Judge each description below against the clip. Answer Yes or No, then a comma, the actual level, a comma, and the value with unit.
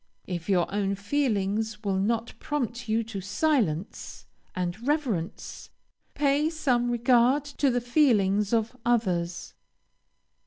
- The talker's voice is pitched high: Yes, high, 230 Hz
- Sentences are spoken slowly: Yes, slow, 115 wpm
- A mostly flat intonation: No, average, 4.5 semitones